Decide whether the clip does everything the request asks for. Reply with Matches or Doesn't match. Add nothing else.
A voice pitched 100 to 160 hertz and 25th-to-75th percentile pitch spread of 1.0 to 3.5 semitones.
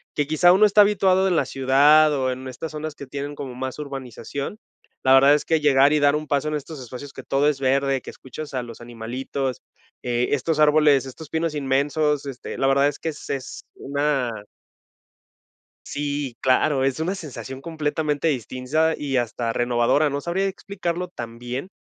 Matches